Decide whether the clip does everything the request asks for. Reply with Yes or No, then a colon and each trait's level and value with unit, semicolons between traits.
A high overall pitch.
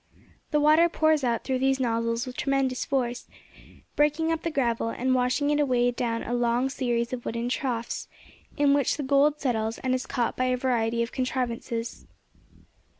Yes: very high, 255 Hz